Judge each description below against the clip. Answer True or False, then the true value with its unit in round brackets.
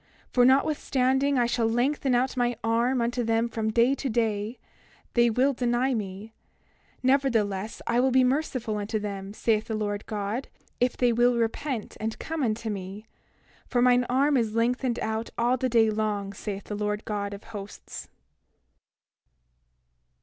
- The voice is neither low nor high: False (235 Hz)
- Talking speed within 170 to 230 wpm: False (155 wpm)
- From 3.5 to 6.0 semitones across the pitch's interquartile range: False (2.8 semitones)